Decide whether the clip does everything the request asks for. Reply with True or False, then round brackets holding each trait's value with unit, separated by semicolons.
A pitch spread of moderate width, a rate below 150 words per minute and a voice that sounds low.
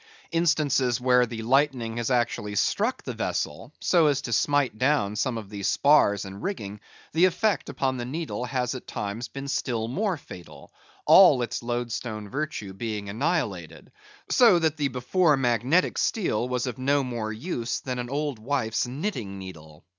False (4.7 semitones; 165 wpm; 125 Hz)